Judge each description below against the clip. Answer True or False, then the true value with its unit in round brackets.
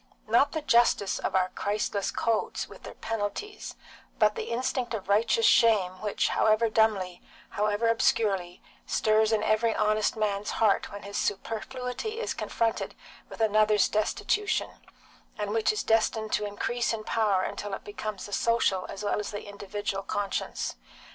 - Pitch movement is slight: True (2.0 semitones)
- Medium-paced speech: True (155 wpm)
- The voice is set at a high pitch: True (215 Hz)